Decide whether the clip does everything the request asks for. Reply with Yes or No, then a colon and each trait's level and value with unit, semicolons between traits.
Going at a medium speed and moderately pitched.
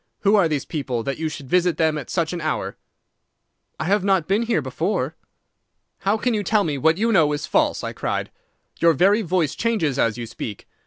No: fast, 210 wpm; medium, 165 Hz